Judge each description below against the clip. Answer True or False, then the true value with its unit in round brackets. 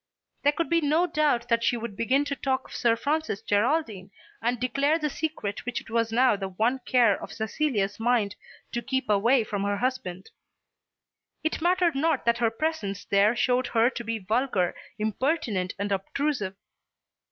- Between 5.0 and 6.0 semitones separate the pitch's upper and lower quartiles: True (5.4 semitones)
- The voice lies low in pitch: False (240 Hz)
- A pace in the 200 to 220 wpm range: False (175 wpm)